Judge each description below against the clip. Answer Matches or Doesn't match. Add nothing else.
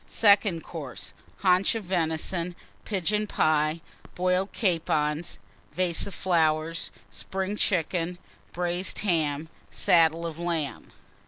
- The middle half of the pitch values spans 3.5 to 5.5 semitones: Doesn't match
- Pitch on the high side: Doesn't match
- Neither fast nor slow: Doesn't match